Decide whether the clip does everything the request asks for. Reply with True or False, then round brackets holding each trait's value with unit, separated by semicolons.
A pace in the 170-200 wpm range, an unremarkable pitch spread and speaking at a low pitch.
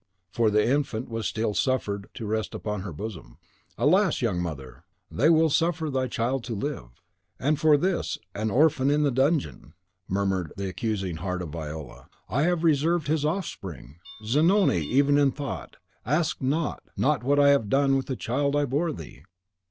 False (175 wpm; 6.6 semitones; 130 Hz)